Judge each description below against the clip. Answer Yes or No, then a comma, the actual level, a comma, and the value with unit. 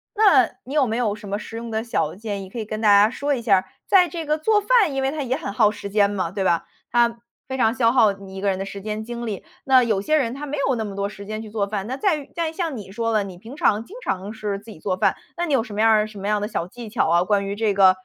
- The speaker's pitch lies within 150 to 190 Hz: No, high, 220 Hz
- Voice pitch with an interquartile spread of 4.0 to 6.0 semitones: Yes, average, 4.5 semitones